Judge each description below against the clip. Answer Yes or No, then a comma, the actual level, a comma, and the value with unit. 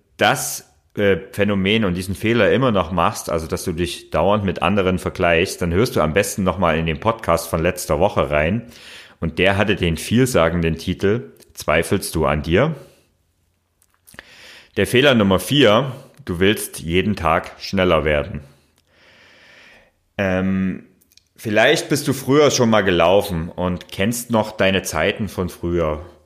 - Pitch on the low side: Yes, very low, 95 Hz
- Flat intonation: No, average, 3.3 semitones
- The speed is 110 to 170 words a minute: Yes, average, 150 wpm